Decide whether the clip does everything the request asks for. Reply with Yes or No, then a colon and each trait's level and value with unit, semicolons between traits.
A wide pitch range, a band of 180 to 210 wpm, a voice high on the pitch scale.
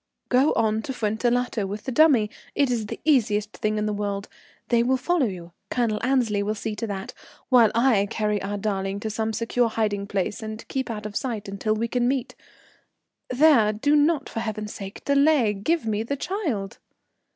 No: average, 3.4 semitones; average, 190 wpm; high, 220 Hz